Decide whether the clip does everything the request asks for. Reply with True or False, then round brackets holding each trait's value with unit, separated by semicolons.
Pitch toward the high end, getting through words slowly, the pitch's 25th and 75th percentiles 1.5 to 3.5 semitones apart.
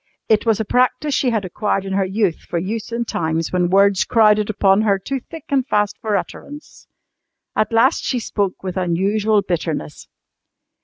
False (210 Hz; 175 wpm; 3.2 semitones)